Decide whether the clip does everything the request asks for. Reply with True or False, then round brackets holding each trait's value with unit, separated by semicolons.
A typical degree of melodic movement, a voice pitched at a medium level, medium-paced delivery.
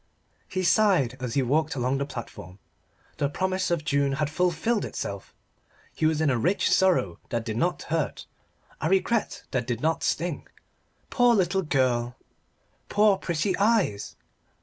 False (6.6 semitones; 155 Hz; 150 wpm)